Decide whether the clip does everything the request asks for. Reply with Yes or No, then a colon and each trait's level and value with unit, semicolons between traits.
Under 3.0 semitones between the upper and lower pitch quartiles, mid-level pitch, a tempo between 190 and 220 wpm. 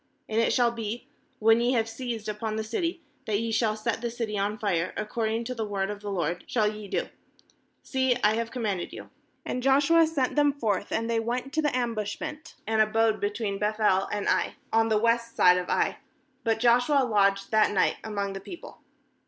No: narrow, 2.4 semitones; high, 225 Hz; fast, 205 wpm